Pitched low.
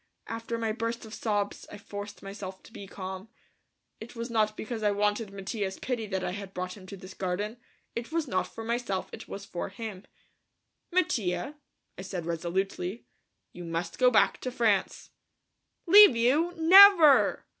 No: high, 210 Hz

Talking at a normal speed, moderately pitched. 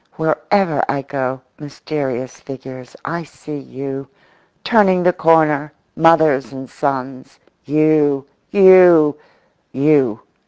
No: slow, 95 wpm; medium, 145 Hz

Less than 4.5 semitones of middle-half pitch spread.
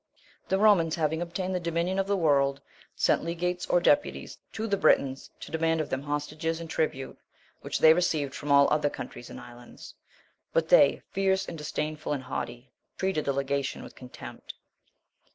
Yes: average, 4.1 semitones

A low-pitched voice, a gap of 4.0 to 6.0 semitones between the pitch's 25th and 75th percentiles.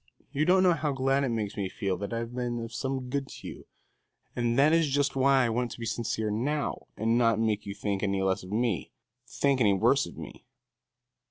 Yes: low, 120 Hz; average, 4.3 semitones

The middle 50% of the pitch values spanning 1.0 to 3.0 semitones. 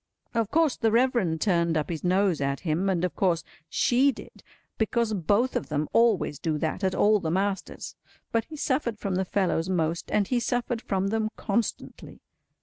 No: average, 5.3 semitones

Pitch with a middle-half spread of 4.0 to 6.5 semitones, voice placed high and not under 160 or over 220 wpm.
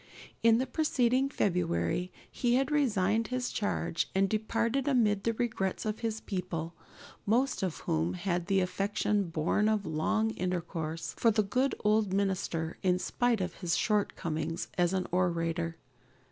No: average, 4.7 semitones; high, 200 Hz; average, 145 wpm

